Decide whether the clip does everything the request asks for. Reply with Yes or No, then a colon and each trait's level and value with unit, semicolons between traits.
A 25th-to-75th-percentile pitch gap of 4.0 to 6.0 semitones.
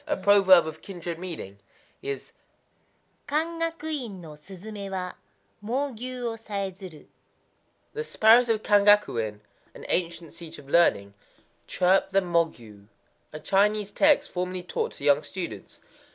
Yes: average, 5.2 semitones